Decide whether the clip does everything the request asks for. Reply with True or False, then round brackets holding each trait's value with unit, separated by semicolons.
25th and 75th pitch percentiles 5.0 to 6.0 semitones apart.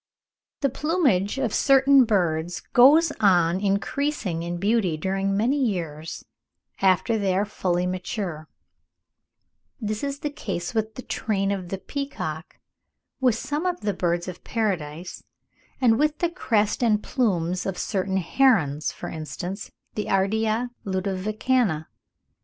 True (5.5 semitones)